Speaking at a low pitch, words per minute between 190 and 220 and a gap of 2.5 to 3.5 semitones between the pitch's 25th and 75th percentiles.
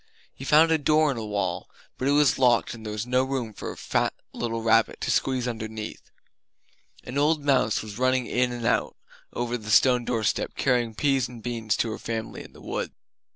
Yes: low, 120 Hz; fast, 205 wpm; average, 2.9 semitones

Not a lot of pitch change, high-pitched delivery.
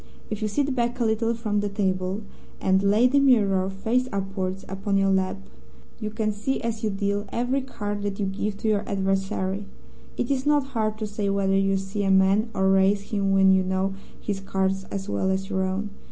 Yes: narrow, 2.1 semitones; high, 200 Hz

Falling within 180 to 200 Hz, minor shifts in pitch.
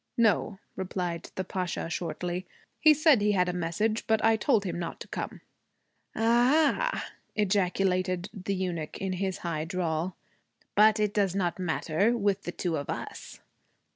No: high, 190 Hz; average, 3.3 semitones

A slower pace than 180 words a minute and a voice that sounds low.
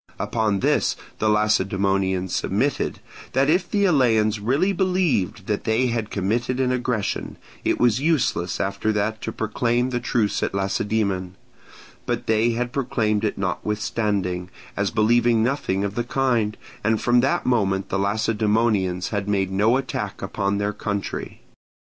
Yes: average, 145 wpm; low, 110 Hz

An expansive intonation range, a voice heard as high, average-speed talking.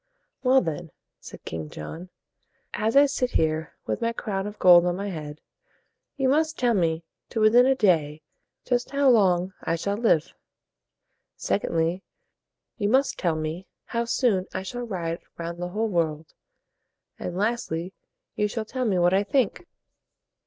Yes: wide, 5.9 semitones; high, 195 Hz; average, 165 wpm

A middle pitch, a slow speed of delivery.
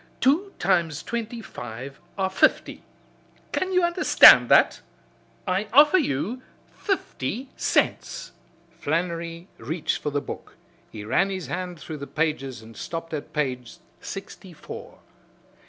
Yes: medium, 170 Hz; slow, 125 wpm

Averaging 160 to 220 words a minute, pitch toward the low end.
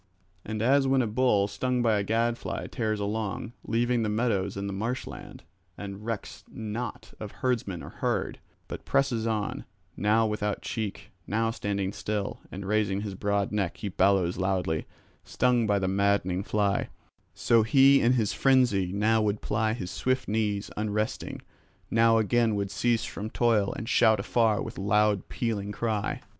Yes: average, 165 wpm; low, 105 Hz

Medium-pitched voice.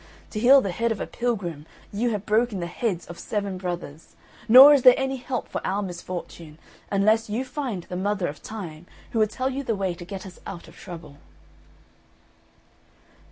No: high, 200 Hz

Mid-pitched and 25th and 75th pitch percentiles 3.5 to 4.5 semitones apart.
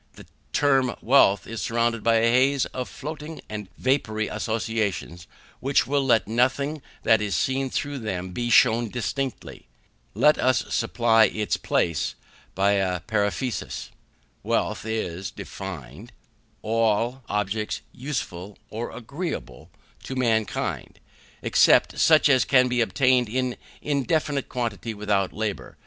No: low, 115 Hz; average, 4.0 semitones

